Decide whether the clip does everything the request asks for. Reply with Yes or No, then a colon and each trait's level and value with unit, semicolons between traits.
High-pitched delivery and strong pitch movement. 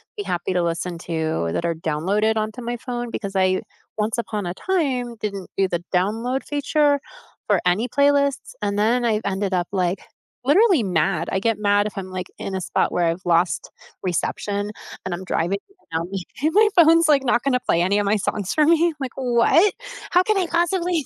Yes: high, 210 Hz; wide, 7.0 semitones